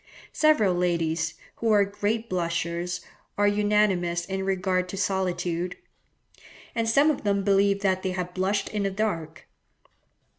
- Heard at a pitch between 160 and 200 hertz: Yes, high, 190 Hz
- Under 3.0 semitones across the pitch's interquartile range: Yes, narrow, 2.6 semitones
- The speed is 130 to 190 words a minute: Yes, average, 140 wpm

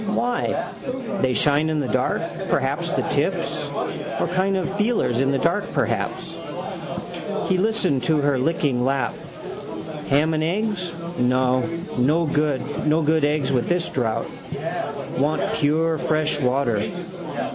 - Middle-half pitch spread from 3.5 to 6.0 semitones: Yes, average, 4.2 semitones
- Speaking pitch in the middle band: Yes, medium, 150 Hz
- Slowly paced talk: Yes, slow, 125 wpm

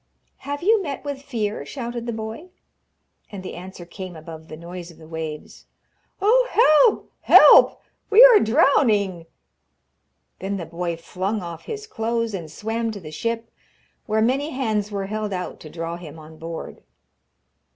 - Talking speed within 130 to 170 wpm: Yes, average, 160 wpm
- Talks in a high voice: Yes, high, 210 Hz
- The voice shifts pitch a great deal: Yes, wide, 7.0 semitones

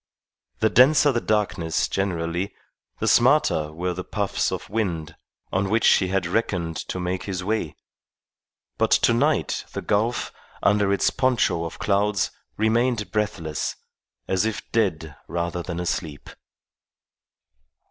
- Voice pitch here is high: No, very low, 95 Hz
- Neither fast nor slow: No, slow, 125 wpm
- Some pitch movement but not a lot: Yes, average, 4.2 semitones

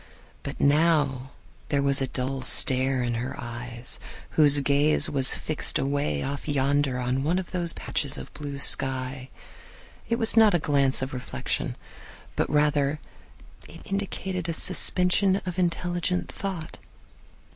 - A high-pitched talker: No, medium, 140 Hz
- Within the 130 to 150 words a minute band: Yes, slow, 135 wpm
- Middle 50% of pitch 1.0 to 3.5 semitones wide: No, average, 4.3 semitones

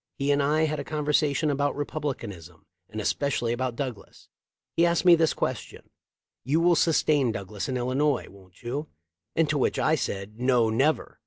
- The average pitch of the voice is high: No, medium, 140 Hz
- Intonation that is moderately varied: Yes, average, 4.6 semitones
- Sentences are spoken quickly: No, average, 175 wpm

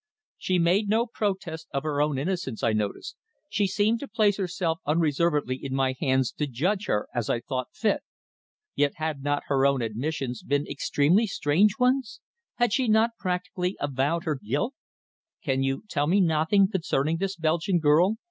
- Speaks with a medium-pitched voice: Yes, medium, 160 Hz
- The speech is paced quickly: No, average, 170 wpm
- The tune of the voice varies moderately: No, wide, 5.9 semitones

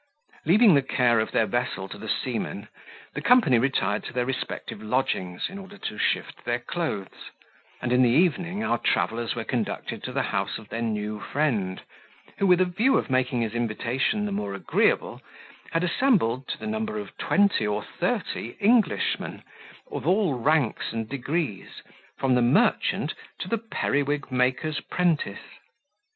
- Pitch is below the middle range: Yes, low, 130 Hz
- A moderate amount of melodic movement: No, wide, 7.8 semitones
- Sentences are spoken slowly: No, average, 165 wpm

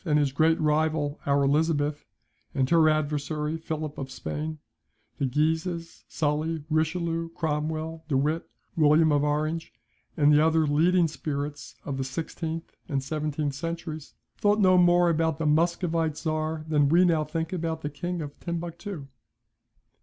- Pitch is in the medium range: Yes, medium, 155 Hz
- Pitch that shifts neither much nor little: No, narrow, 1.9 semitones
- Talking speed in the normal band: Yes, average, 145 wpm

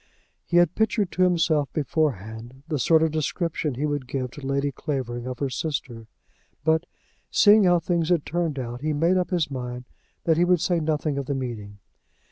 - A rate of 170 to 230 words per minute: Yes, average, 190 wpm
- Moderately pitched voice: Yes, medium, 150 Hz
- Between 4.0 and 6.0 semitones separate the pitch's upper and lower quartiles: Yes, average, 4.6 semitones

